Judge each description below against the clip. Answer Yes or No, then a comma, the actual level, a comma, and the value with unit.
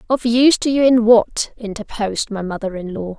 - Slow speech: No, fast, 205 wpm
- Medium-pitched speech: No, high, 220 Hz